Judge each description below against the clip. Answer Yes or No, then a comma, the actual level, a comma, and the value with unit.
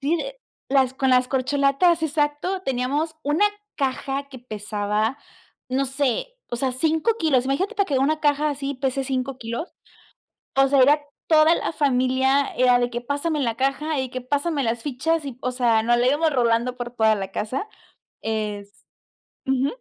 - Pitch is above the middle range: Yes, very high, 270 Hz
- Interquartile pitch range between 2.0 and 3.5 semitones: Yes, average, 3.0 semitones